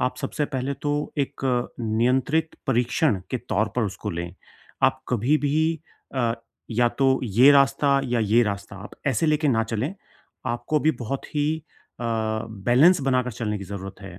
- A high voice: No, low, 125 Hz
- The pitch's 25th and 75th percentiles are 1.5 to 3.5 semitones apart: No, average, 4.2 semitones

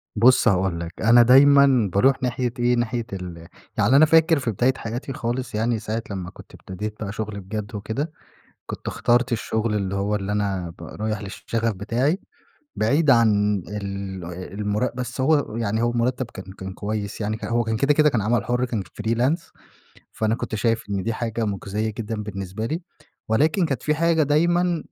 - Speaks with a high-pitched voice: No, low, 115 Hz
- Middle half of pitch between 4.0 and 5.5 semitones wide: No, average, 3.6 semitones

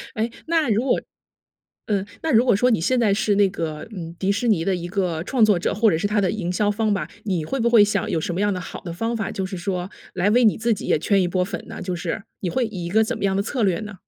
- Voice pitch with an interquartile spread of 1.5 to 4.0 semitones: Yes, average, 3.5 semitones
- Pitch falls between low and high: No, high, 200 Hz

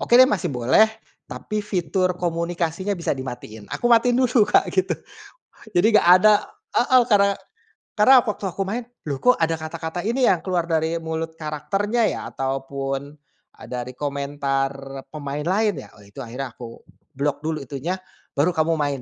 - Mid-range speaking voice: Yes, medium, 165 Hz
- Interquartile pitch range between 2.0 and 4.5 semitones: No, wide, 6.5 semitones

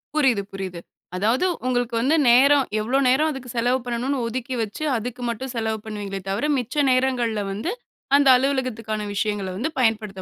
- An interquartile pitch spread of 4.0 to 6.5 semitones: No, average, 3.5 semitones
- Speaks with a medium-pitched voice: No, high, 240 Hz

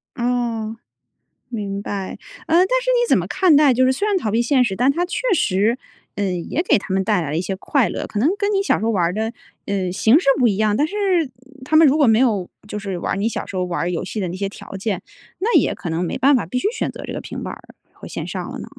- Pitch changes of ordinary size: No, wide, 6.3 semitones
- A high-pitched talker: Yes, high, 220 Hz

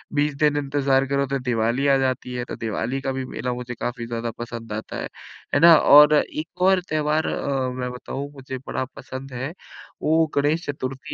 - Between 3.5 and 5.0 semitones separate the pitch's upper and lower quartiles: No, average, 2.7 semitones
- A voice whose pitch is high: No, low, 135 Hz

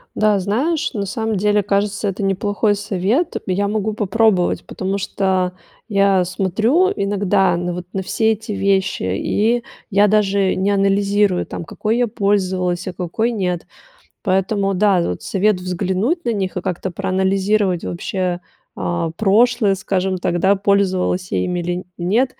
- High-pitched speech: Yes, high, 195 Hz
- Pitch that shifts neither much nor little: No, narrow, 2.2 semitones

